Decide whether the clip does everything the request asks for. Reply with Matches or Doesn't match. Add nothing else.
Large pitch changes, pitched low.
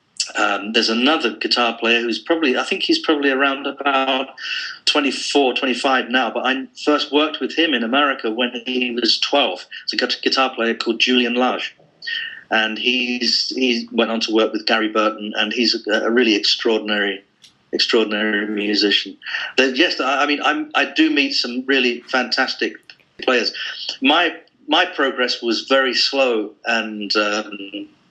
Doesn't match